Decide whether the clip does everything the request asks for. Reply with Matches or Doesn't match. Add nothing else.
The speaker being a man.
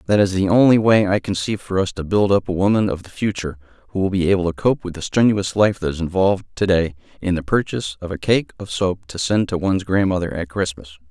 Matches